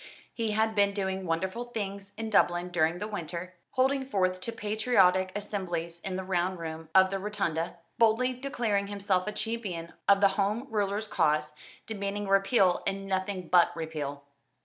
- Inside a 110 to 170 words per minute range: Yes, average, 160 wpm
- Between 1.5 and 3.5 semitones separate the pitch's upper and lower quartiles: Yes, average, 3.0 semitones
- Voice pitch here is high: Yes, high, 195 Hz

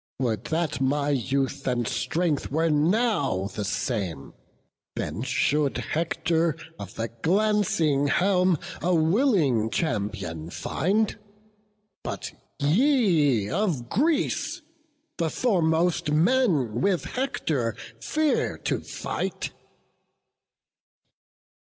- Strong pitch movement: Yes, wide, 6.7 semitones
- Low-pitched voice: No, medium, 155 Hz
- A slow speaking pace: Yes, slow, 95 wpm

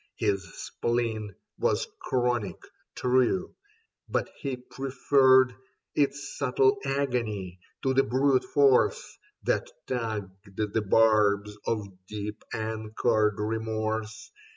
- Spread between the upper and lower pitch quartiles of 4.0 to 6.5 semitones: No, average, 3.5 semitones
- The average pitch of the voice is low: Yes, low, 110 Hz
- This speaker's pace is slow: Yes, slow, 95 wpm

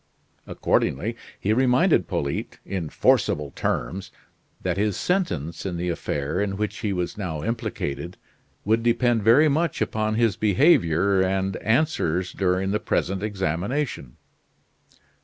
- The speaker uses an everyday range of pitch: Yes, average, 4.5 semitones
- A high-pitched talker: No, low, 100 Hz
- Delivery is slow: Yes, slow, 125 wpm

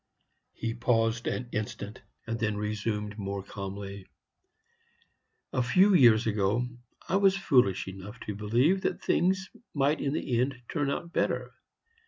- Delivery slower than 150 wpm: Yes, average, 140 wpm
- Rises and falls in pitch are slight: No, average, 5.1 semitones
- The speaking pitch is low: Yes, low, 115 Hz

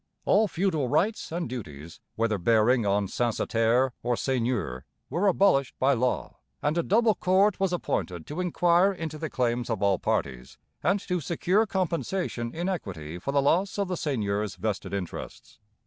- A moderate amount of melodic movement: No, wide, 8.9 semitones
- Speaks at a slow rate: No, average, 165 wpm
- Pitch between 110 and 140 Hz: Yes, low, 135 Hz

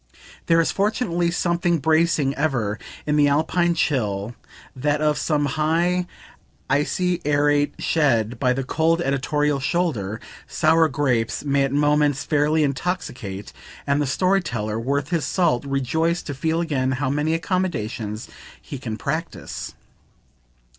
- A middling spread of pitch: Yes, average, 3.8 semitones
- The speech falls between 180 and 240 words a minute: No, slow, 135 wpm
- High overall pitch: No, medium, 145 Hz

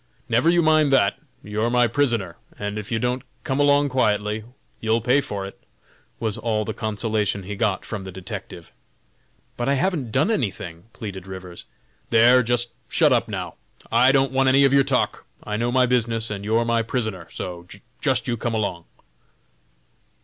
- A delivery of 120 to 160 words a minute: No, average, 175 wpm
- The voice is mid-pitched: No, low, 115 Hz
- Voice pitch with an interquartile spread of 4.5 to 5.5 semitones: No, average, 3.8 semitones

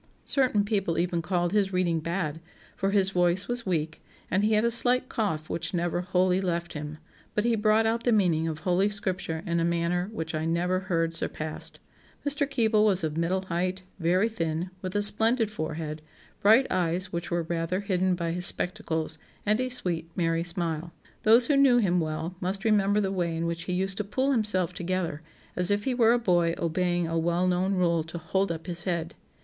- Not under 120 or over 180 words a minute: No, average, 200 wpm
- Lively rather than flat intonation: No, average, 3.5 semitones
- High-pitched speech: No, medium, 180 Hz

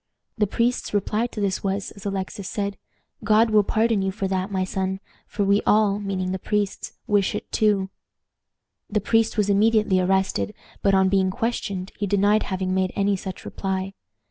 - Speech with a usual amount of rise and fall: No, narrow, 1.8 semitones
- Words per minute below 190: Yes, average, 175 wpm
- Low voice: No, high, 200 Hz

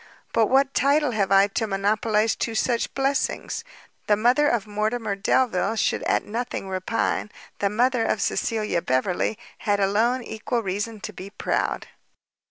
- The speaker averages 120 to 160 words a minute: Yes, average, 150 wpm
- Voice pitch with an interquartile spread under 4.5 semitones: Yes, average, 3.3 semitones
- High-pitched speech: Yes, high, 220 Hz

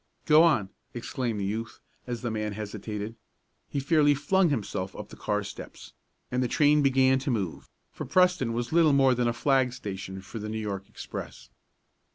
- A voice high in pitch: No, low, 120 Hz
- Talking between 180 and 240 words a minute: Yes, average, 185 wpm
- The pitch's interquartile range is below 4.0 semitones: No, average, 4.8 semitones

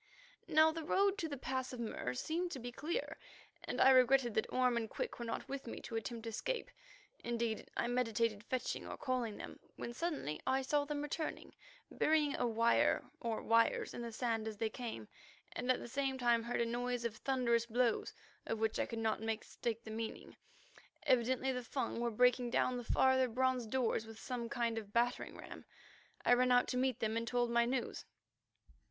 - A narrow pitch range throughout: Yes, narrow, 2.2 semitones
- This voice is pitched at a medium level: No, high, 240 Hz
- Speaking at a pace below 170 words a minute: No, average, 195 wpm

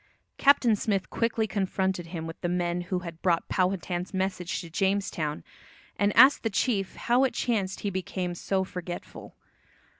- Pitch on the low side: No, high, 190 Hz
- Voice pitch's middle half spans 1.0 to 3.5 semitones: Yes, narrow, 2.5 semitones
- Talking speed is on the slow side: No, average, 155 wpm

